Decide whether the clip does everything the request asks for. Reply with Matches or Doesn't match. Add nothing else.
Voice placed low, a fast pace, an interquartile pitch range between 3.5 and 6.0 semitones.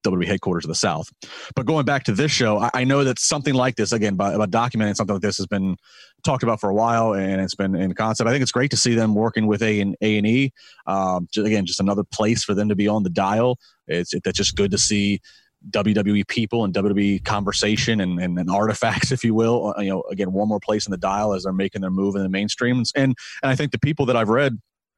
Doesn't match